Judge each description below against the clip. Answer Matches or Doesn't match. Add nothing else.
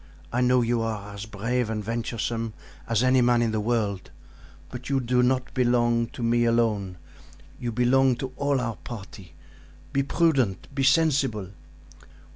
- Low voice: Matches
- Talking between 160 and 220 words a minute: Doesn't match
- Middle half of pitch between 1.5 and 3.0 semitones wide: Matches